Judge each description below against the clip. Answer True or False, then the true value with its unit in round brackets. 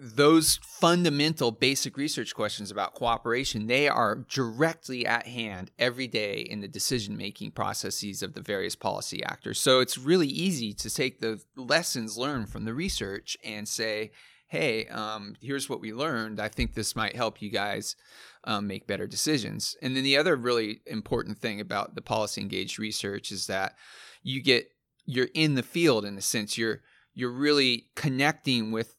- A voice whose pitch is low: True (120 Hz)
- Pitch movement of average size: True (4.2 semitones)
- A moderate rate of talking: True (170 wpm)